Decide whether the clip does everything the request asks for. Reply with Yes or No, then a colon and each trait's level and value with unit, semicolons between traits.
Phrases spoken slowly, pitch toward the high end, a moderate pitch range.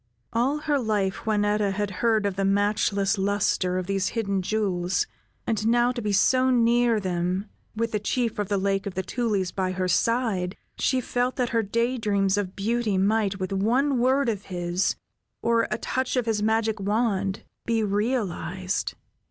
No: average, 175 wpm; high, 210 Hz; average, 3.2 semitones